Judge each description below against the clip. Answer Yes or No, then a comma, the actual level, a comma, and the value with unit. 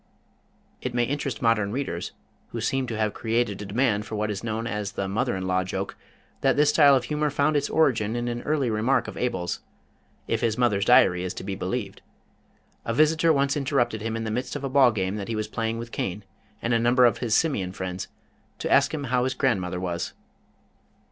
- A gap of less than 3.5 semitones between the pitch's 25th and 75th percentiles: No, average, 4.3 semitones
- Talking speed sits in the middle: No, fast, 215 wpm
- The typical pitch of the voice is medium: No, low, 115 Hz